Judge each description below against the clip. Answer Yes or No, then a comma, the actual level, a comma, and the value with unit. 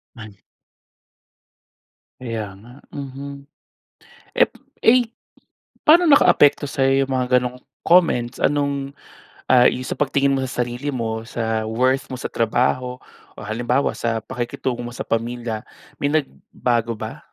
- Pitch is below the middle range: Yes, low, 125 Hz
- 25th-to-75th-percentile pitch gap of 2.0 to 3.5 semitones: Yes, average, 2.9 semitones